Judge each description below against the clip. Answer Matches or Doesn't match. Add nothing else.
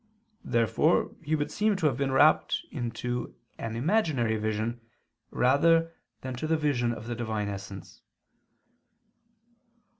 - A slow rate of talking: Matches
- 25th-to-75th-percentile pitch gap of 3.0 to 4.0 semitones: Doesn't match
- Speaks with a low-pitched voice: Matches